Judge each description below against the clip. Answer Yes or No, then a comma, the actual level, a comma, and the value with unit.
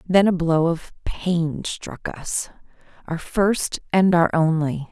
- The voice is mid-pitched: Yes, medium, 170 Hz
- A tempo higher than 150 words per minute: No, average, 145 wpm